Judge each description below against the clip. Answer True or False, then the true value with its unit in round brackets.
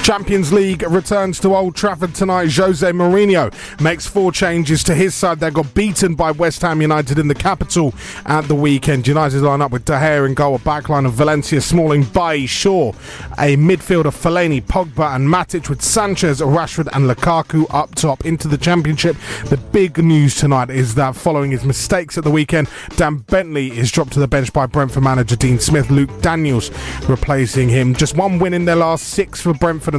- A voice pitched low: False (155 Hz)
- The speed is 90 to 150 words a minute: False (195 wpm)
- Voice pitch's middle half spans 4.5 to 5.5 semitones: False (3.8 semitones)